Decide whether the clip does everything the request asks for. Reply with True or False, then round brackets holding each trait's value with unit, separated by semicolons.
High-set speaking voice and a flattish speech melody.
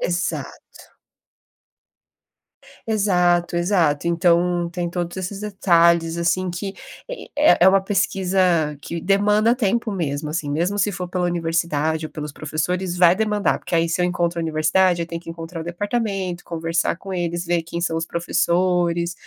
False (175 Hz; 2.1 semitones)